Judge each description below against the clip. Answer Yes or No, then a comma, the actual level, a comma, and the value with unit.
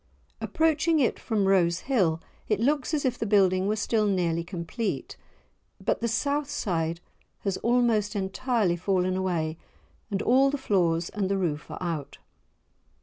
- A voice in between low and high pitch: No, high, 200 Hz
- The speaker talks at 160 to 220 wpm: No, average, 150 wpm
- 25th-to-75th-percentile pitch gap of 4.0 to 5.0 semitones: No, wide, 5.5 semitones